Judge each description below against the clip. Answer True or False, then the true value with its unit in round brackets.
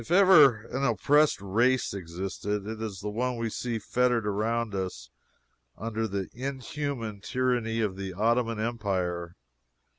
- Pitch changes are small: False (3.8 semitones)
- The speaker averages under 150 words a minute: True (140 wpm)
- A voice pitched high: False (110 Hz)